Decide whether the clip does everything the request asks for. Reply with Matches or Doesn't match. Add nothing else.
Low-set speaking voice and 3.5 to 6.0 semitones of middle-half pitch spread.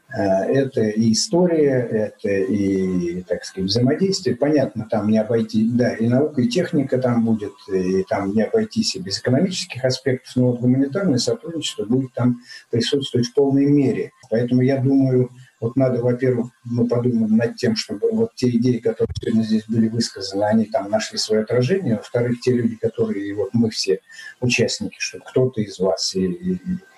Matches